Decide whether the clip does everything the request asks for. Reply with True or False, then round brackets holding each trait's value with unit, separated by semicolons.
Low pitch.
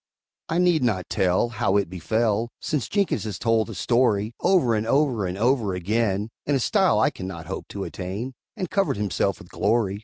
True (110 Hz)